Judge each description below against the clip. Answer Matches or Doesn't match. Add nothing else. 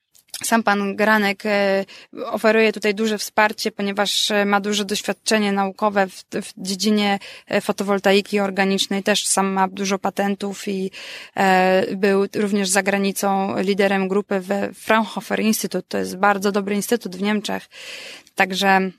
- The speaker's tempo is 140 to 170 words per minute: Doesn't match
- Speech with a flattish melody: Matches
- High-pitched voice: Matches